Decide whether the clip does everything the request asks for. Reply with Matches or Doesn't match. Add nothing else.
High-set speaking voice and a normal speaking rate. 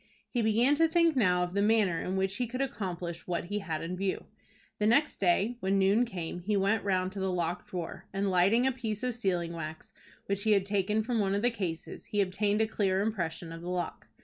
Doesn't match